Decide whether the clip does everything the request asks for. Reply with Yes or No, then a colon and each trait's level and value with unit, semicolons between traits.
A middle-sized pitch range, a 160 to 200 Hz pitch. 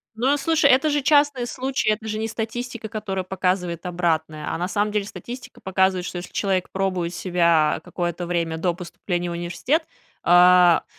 Yes: average, 4.6 semitones; high, 190 Hz